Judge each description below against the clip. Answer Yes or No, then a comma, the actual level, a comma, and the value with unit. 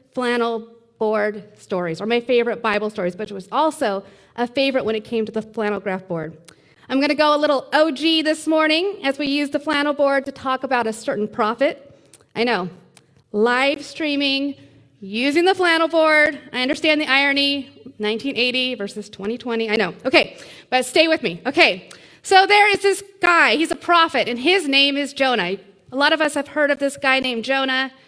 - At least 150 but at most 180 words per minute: No, average, 190 wpm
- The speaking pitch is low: No, very high, 260 Hz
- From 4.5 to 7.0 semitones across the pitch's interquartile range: Yes, wide, 5.4 semitones